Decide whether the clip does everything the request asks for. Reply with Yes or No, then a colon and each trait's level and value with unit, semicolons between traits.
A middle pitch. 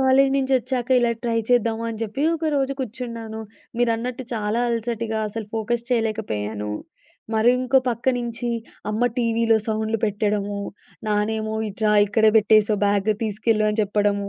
No: high, 225 Hz